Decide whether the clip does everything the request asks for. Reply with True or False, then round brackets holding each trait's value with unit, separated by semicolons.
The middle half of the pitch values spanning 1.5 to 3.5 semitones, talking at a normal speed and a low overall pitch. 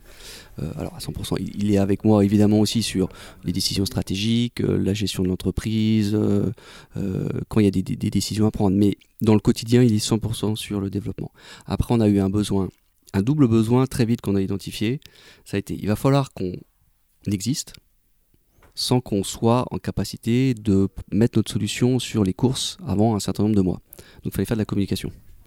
True (2.8 semitones; 200 wpm; 105 Hz)